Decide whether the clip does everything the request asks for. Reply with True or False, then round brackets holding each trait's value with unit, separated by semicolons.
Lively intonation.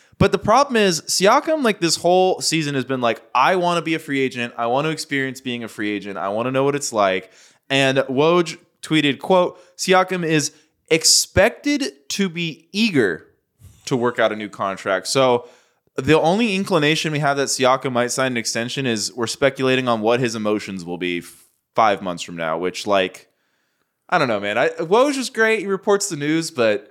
True (6.7 semitones)